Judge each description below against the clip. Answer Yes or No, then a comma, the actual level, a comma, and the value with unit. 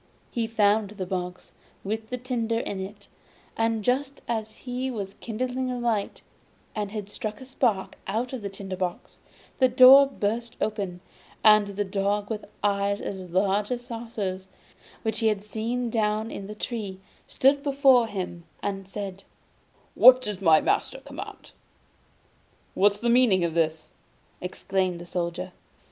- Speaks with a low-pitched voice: No, high, 210 Hz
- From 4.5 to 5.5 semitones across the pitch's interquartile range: No, average, 3.5 semitones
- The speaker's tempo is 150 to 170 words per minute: Yes, average, 155 wpm